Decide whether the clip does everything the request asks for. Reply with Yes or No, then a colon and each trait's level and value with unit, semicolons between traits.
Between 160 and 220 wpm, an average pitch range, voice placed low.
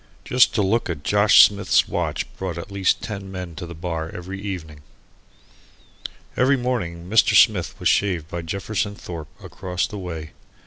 Yes: average, 165 wpm; average, 3.2 semitones; very low, 95 Hz